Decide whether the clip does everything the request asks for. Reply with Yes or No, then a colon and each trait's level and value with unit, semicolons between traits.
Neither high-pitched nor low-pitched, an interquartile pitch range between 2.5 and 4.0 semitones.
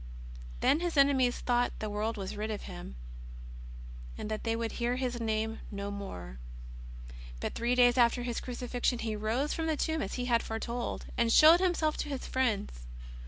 No: high, 235 Hz; average, 3.1 semitones